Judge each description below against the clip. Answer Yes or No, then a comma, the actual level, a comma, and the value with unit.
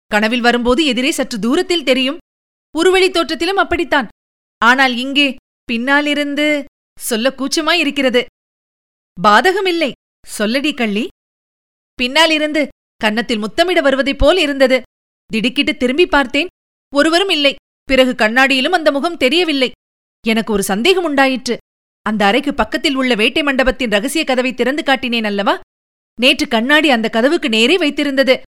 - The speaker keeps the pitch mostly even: No, average, 3.7 semitones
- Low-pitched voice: No, very high, 275 Hz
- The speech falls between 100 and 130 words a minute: Yes, average, 110 wpm